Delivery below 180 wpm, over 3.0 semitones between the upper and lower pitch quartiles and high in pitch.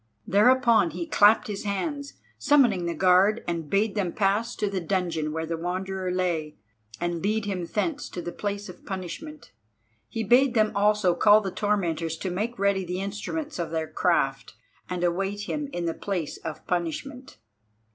Yes: average, 170 wpm; average, 3.6 semitones; high, 195 Hz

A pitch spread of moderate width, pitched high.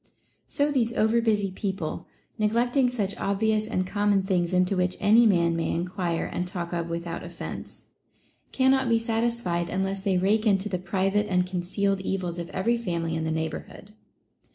Yes: average, 3.6 semitones; high, 195 Hz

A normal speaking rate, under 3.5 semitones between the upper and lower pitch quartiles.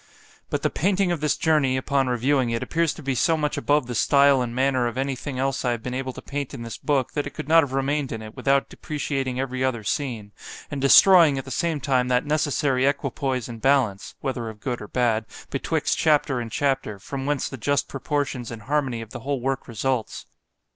No: fast, 225 wpm; narrow, 2.6 semitones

